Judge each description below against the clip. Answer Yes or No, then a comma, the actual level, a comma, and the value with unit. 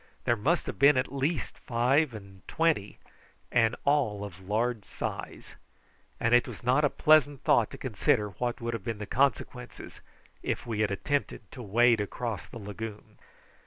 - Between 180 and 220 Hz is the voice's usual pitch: No, low, 120 Hz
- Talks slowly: No, average, 165 wpm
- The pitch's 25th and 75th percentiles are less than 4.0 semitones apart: No, average, 4.6 semitones